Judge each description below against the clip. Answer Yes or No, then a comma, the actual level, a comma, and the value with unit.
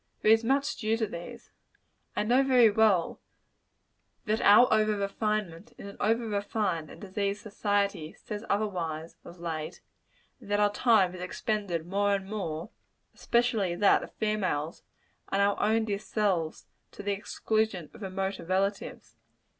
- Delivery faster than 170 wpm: No, average, 150 wpm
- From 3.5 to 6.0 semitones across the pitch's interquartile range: No, average, 2.8 semitones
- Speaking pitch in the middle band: No, high, 205 Hz